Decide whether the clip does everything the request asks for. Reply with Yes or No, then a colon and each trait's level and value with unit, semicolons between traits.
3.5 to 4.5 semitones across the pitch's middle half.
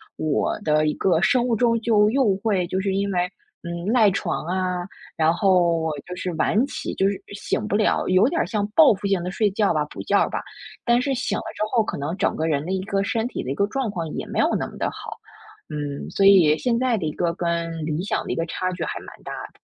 Yes: average, 4.2 semitones